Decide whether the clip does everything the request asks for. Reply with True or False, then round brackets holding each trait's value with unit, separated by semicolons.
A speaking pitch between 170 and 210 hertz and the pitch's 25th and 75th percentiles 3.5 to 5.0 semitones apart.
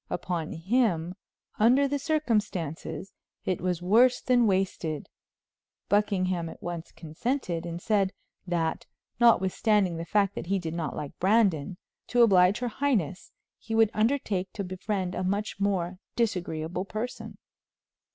True (190 Hz; 4.2 semitones)